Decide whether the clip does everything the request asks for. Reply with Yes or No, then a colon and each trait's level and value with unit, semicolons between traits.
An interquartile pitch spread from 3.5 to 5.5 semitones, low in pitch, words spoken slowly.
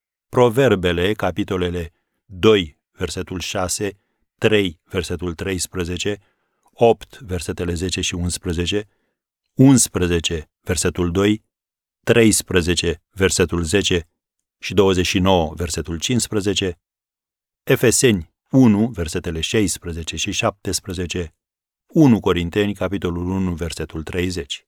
No: average, 2.8 semitones; very low, 90 Hz; slow, 85 wpm